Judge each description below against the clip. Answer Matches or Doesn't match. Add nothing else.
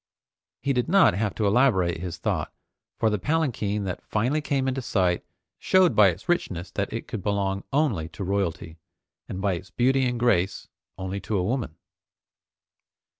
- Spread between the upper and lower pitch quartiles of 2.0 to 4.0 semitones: Doesn't match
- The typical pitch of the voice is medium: Doesn't match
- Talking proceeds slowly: Doesn't match